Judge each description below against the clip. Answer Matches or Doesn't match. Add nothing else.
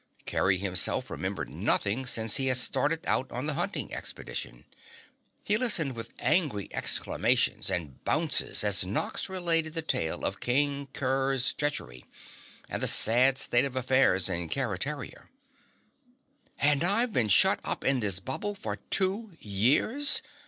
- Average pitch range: Doesn't match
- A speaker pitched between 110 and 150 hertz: Matches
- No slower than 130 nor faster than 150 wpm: Matches